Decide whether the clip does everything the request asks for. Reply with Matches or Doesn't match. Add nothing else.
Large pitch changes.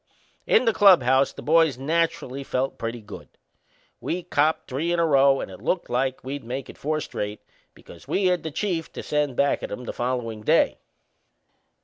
Doesn't match